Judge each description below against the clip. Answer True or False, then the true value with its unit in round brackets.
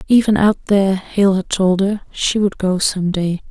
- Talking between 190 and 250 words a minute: True (205 wpm)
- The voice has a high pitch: True (195 Hz)